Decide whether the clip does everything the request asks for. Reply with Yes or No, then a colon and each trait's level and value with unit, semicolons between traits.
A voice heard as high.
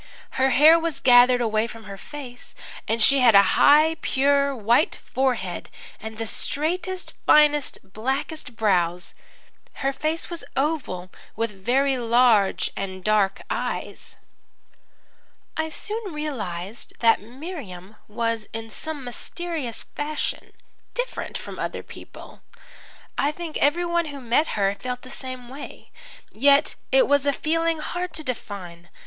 Yes: very high, 260 Hz